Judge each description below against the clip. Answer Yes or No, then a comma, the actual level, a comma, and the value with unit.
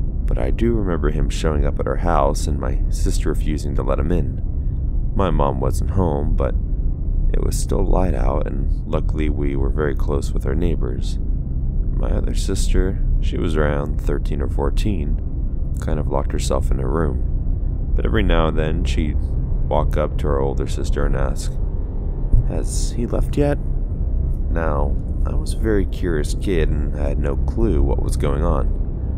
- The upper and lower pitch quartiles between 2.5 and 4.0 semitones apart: Yes, average, 3.6 semitones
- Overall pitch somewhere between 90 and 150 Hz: No, very low, 75 Hz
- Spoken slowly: No, average, 175 wpm